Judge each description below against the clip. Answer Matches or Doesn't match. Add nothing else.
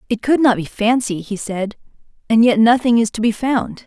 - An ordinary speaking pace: Doesn't match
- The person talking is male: Doesn't match